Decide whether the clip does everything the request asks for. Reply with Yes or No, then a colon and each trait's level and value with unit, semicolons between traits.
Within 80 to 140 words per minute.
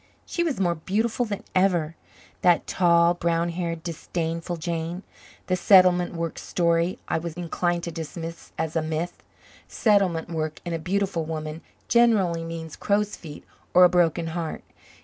No: average, 150 wpm